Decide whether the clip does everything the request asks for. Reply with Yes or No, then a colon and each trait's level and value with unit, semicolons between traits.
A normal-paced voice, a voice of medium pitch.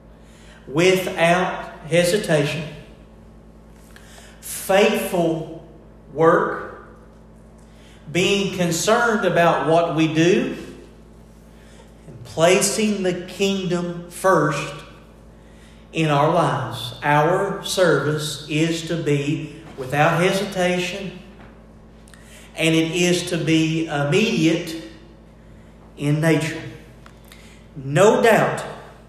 No: slow, 70 wpm; medium, 170 Hz